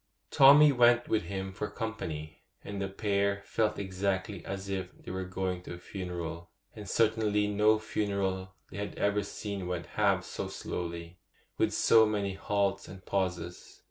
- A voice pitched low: Yes, low, 100 Hz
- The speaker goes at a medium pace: Yes, average, 165 wpm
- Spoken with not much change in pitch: Yes, narrow, 2.1 semitones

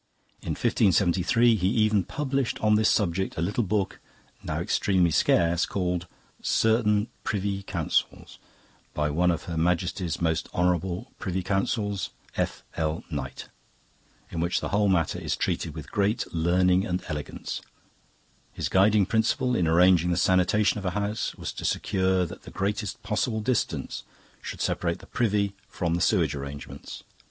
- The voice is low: Yes, very low, 95 Hz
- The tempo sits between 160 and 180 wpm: No, average, 145 wpm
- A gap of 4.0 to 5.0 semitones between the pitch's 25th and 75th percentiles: No, average, 3.4 semitones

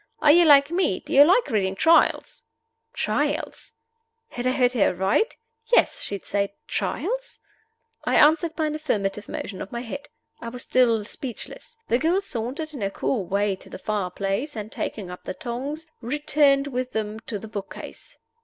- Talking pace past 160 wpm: Yes, average, 180 wpm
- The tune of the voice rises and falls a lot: Yes, wide, 6.6 semitones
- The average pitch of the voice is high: Yes, high, 245 Hz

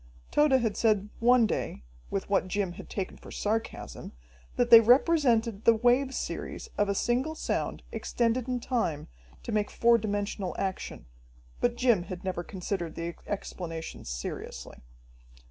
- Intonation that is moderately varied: Yes, average, 4.2 semitones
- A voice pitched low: No, high, 215 Hz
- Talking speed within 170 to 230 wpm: No, average, 145 wpm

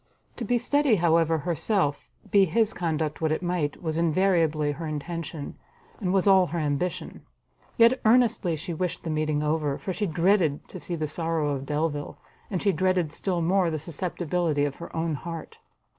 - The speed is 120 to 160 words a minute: No, average, 175 wpm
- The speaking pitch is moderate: Yes, medium, 165 Hz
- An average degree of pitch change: Yes, average, 3.3 semitones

